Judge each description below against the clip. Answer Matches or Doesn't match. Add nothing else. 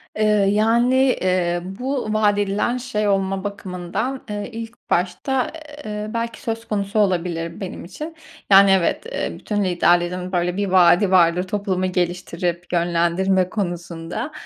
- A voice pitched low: Doesn't match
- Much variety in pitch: Doesn't match